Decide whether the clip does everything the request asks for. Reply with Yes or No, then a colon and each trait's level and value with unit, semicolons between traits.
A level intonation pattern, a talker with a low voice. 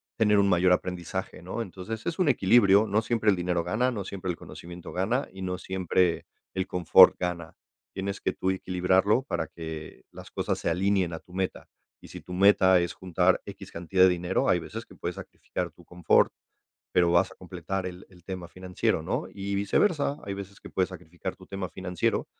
Yes: narrow, 1.9 semitones; very low, 95 Hz